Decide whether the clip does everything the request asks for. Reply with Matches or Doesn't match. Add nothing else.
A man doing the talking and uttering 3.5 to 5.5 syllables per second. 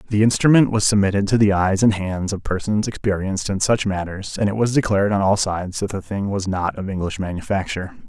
Doesn't match